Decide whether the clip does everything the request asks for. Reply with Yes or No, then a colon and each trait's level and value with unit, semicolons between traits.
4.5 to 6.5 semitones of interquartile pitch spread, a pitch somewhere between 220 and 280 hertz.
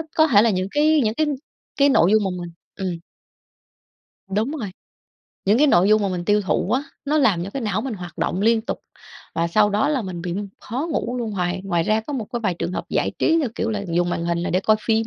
No: average, 4.9 semitones; high, 210 Hz